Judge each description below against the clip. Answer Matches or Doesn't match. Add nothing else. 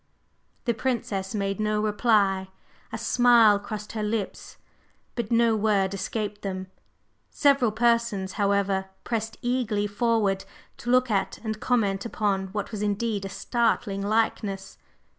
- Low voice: Doesn't match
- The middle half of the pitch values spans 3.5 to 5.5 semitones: Doesn't match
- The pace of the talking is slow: Matches